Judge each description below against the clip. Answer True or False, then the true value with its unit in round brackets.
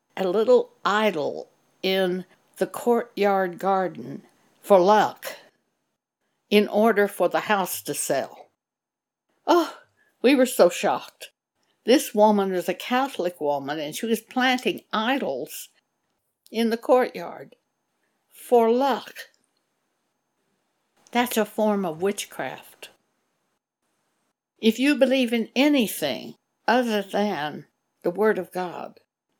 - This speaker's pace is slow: True (110 wpm)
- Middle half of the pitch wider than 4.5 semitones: True (5.0 semitones)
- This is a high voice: True (215 Hz)